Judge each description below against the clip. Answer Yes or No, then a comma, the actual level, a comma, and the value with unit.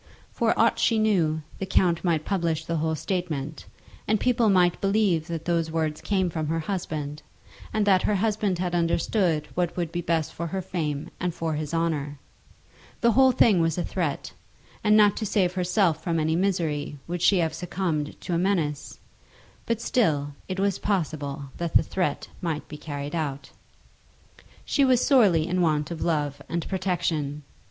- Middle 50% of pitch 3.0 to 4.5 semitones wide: Yes, average, 3.5 semitones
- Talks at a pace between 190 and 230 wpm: No, average, 175 wpm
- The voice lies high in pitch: No, medium, 170 Hz